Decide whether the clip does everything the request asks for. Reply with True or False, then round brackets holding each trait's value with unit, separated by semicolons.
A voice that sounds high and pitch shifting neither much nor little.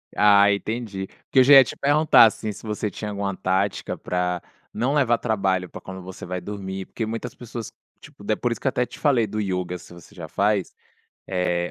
False (100 Hz; 3.7 semitones)